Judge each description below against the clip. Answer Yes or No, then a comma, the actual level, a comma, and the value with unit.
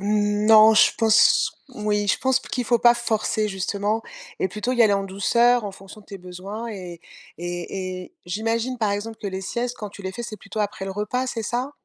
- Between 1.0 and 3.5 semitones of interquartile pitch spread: Yes, average, 2.9 semitones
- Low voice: No, high, 210 Hz